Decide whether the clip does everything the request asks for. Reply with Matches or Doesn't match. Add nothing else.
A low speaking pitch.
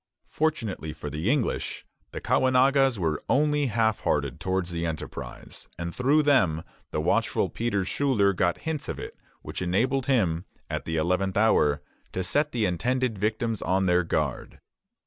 Matches